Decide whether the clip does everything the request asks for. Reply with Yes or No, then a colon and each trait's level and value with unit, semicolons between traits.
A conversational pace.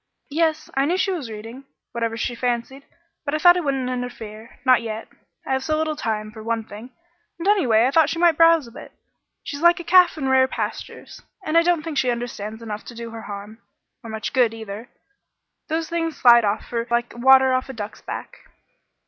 No: fast, 215 wpm